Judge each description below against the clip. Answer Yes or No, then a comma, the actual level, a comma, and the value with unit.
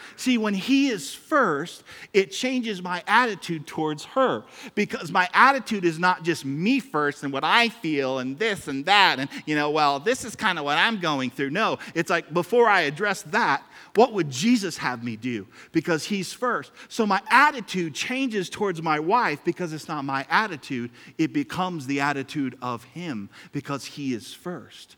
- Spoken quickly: No, average, 185 wpm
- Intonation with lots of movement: Yes, wide, 6.8 semitones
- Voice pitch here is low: No, medium, 170 Hz